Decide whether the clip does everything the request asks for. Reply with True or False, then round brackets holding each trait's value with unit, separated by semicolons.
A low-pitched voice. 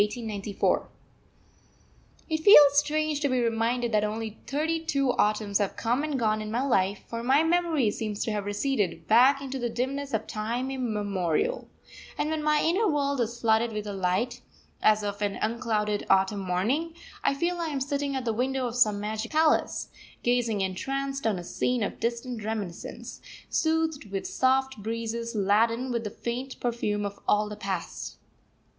False (235 Hz)